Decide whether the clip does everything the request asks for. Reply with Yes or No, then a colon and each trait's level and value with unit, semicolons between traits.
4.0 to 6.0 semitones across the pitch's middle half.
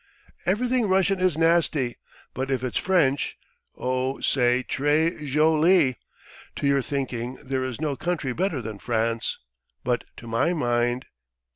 Yes: average, 4.9 semitones